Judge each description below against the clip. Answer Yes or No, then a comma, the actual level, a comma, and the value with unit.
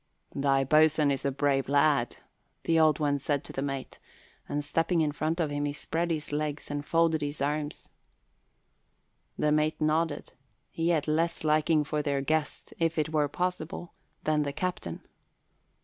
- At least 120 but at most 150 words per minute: No, average, 165 wpm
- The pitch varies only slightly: Yes, narrow, 1.7 semitones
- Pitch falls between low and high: Yes, medium, 150 Hz